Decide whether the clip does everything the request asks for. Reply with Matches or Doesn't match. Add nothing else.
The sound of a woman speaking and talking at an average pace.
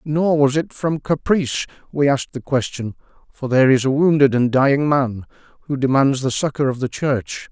Doesn't match